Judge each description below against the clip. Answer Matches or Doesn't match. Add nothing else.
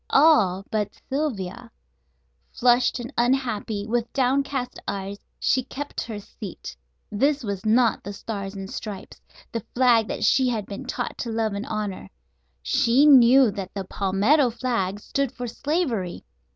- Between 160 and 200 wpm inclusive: Doesn't match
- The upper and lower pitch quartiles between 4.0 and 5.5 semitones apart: Matches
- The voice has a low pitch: Doesn't match